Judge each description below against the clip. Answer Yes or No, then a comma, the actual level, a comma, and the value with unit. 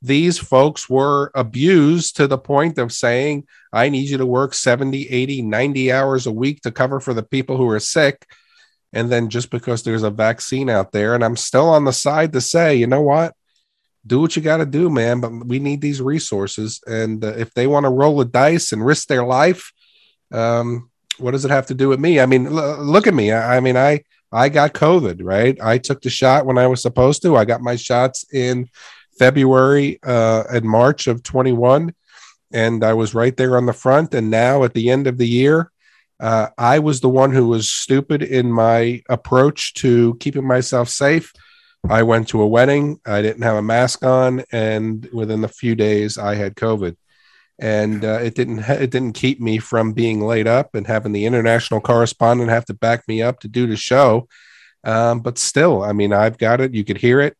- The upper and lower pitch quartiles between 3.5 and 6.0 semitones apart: No, average, 3.1 semitones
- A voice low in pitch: Yes, low, 125 Hz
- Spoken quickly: Yes, fast, 215 wpm